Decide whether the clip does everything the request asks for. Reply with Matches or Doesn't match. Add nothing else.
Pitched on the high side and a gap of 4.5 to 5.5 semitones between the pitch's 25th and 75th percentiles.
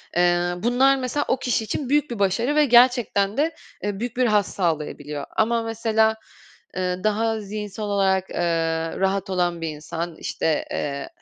Matches